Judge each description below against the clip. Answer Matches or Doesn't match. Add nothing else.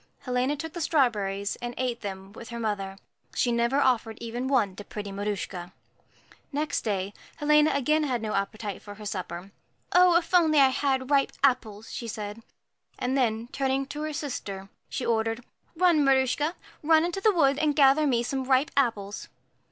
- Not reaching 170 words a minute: Doesn't match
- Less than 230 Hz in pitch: Doesn't match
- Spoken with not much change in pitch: Doesn't match